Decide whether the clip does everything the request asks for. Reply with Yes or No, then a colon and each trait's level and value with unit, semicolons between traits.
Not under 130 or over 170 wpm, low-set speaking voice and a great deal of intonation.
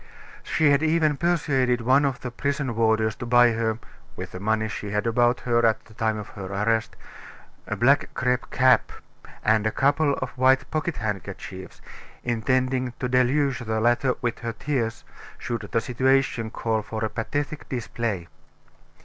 No: average, 165 wpm; low, 120 Hz; average, 3.1 semitones